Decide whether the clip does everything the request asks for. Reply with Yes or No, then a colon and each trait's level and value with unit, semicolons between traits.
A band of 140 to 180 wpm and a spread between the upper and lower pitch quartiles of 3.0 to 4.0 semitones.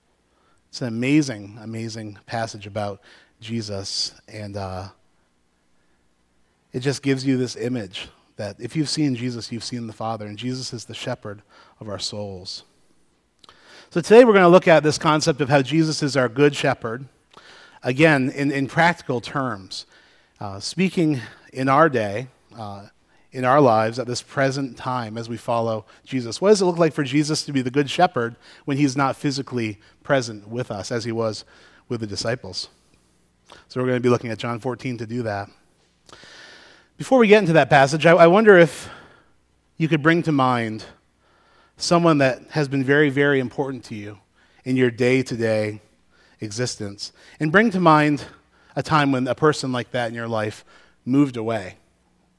No: average, 175 wpm; average, 4.8 semitones